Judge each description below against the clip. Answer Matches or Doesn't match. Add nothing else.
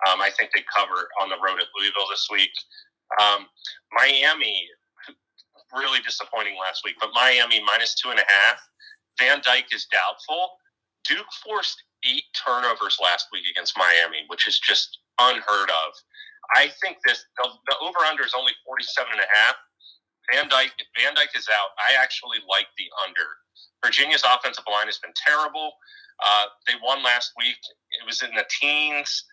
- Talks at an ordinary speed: Matches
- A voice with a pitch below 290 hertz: Doesn't match